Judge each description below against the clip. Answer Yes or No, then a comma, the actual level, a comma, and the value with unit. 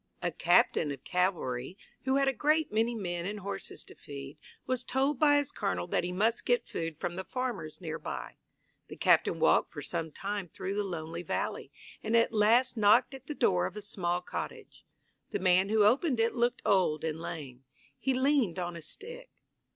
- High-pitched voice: Yes, high, 200 Hz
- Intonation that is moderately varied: No, wide, 6.6 semitones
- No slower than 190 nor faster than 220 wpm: Yes, average, 195 wpm